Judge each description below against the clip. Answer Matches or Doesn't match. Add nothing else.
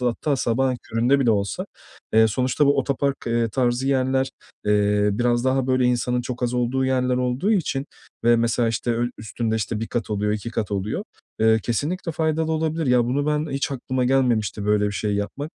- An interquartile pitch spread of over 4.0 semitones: Doesn't match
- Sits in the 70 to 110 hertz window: Doesn't match